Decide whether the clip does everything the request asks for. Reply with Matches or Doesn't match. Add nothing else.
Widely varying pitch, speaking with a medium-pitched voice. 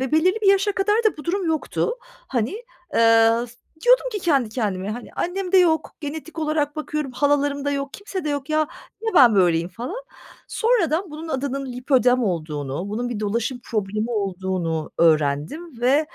Doesn't match